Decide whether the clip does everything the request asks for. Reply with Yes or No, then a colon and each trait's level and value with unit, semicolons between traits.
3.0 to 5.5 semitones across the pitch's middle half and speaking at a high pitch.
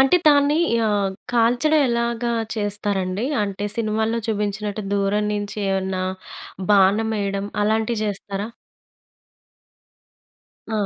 No: narrow, 2.5 semitones; high, 210 Hz